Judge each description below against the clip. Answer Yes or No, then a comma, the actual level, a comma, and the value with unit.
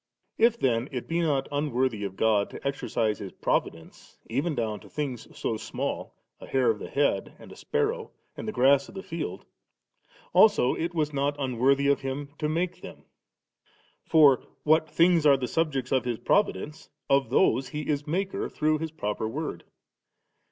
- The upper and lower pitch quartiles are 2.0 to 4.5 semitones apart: Yes, average, 4.2 semitones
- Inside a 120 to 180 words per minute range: Yes, average, 175 wpm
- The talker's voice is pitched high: No, medium, 140 Hz